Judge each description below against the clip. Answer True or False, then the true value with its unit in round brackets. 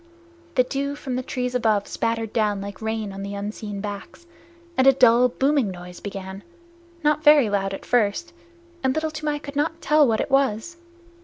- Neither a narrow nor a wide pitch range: False (5.7 semitones)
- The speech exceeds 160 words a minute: True (180 wpm)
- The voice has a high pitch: True (240 Hz)